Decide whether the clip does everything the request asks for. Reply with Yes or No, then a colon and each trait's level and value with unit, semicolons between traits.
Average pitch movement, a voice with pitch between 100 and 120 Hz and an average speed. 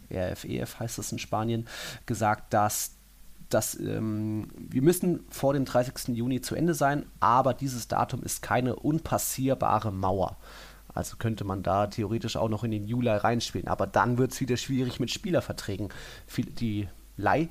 Yes: average, 3.6 semitones; low, 115 Hz; average, 160 wpm